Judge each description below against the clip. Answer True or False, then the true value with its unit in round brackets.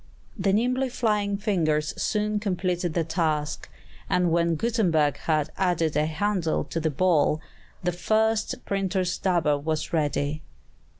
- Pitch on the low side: False (175 Hz)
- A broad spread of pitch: False (4.5 semitones)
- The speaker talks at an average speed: False (130 wpm)